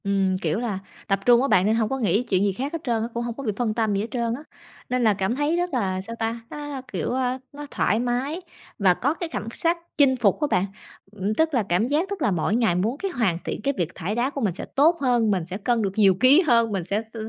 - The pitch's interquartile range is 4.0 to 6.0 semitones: Yes, average, 5.1 semitones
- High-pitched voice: Yes, high, 230 Hz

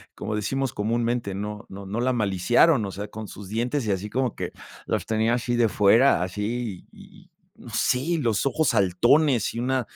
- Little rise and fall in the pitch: No, average, 3.3 semitones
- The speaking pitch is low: Yes, low, 115 Hz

